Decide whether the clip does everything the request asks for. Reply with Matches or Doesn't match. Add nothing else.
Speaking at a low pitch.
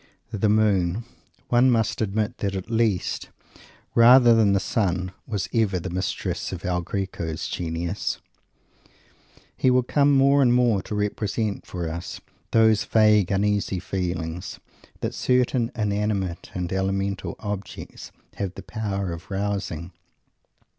Matches